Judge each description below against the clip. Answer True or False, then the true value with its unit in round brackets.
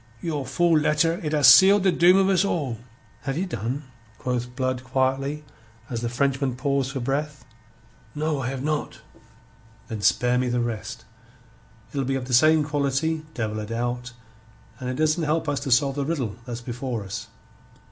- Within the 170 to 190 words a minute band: True (180 wpm)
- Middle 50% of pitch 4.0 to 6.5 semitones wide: False (3.6 semitones)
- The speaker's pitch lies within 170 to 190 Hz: False (135 Hz)